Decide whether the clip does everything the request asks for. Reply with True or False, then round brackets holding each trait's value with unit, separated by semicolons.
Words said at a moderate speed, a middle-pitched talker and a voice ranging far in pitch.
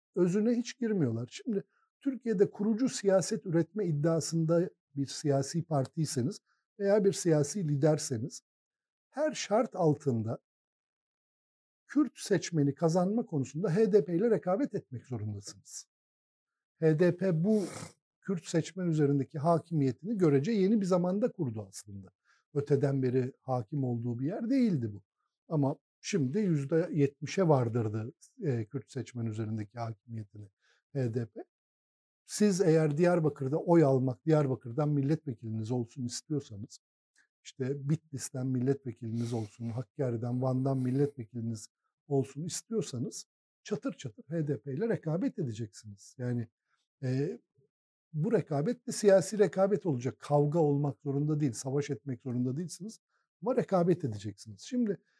True (110 wpm; 145 Hz; 6.5 semitones)